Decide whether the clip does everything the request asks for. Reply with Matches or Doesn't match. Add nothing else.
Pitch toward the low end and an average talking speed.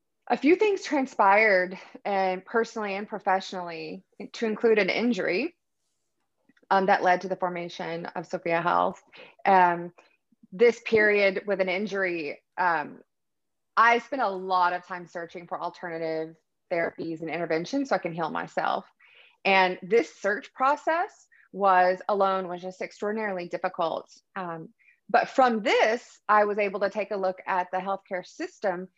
Doesn't match